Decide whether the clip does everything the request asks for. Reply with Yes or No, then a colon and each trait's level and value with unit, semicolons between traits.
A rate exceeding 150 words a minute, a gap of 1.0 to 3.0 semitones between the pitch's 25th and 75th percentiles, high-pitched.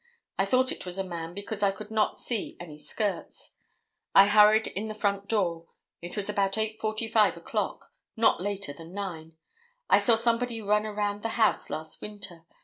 Yes: average, 175 wpm; narrow, 2.5 semitones; high, 205 Hz